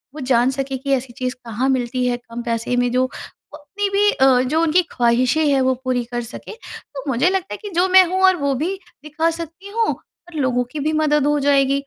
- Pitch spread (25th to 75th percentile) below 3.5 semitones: No, average, 4.4 semitones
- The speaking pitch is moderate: No, very high, 275 Hz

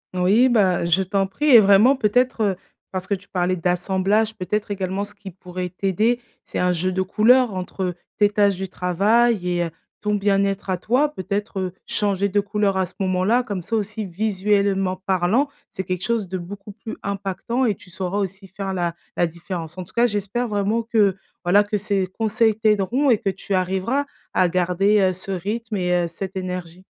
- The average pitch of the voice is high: Yes, high, 195 Hz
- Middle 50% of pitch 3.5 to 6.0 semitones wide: No, narrow, 2.4 semitones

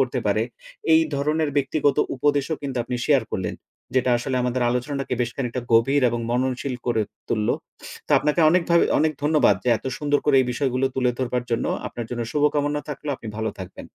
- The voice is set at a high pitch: No, low, 130 Hz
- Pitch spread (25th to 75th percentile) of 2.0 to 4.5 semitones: Yes, average, 3.2 semitones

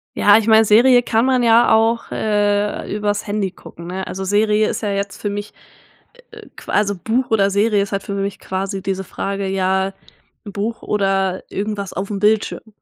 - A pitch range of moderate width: No, narrow, 1.8 semitones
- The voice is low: No, high, 205 Hz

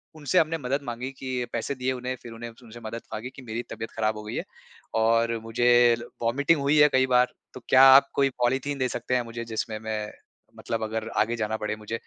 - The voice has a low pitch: Yes, low, 120 Hz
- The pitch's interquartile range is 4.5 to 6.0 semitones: No, average, 2.7 semitones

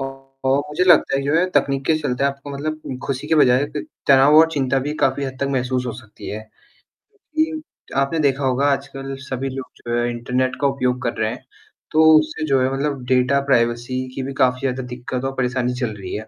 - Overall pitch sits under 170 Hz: Yes, low, 135 Hz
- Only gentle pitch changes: Yes, narrow, 2.0 semitones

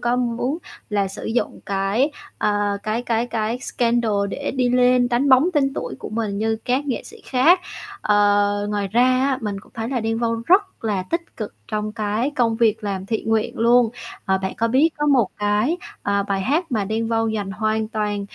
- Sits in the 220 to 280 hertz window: Yes, high, 225 Hz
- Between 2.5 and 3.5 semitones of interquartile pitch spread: Yes, average, 3.2 semitones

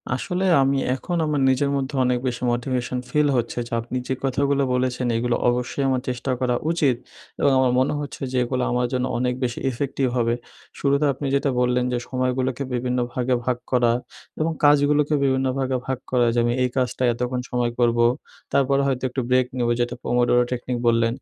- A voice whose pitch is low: Yes, low, 125 Hz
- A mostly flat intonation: Yes, narrow, 1.8 semitones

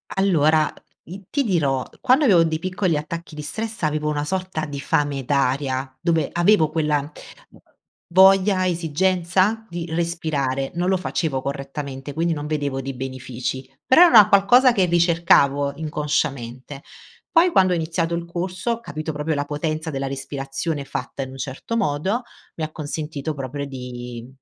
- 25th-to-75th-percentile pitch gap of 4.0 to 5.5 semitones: Yes, average, 4.3 semitones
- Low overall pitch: No, medium, 155 Hz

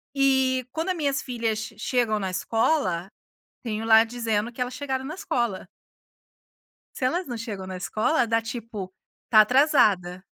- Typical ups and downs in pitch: Yes, average, 3.7 semitones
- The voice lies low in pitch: No, high, 235 Hz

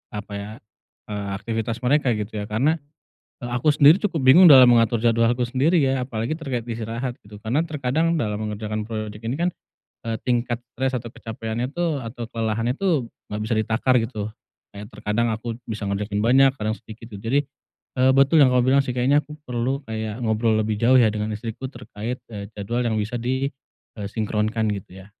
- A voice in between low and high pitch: No, low, 115 Hz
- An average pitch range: Yes, average, 3.2 semitones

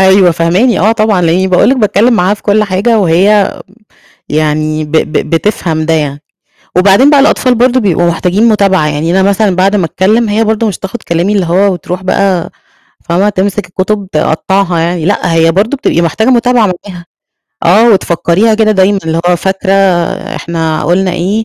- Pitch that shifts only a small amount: No, average, 3.7 semitones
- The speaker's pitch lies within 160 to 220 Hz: Yes, high, 190 Hz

